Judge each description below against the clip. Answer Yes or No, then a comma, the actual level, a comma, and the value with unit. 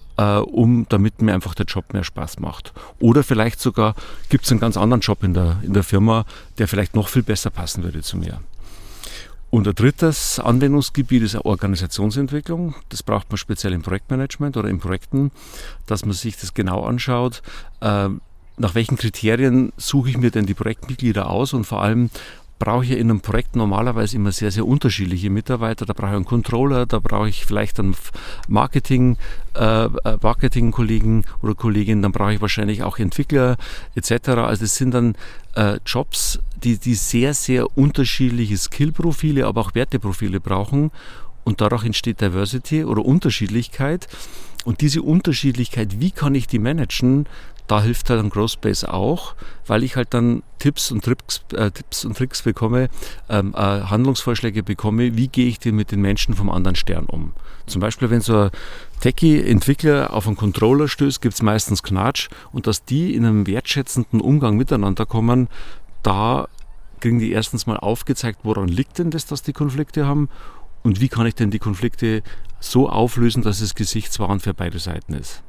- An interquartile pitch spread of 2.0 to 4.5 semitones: Yes, average, 3.7 semitones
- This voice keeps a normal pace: Yes, average, 175 wpm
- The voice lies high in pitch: No, low, 110 Hz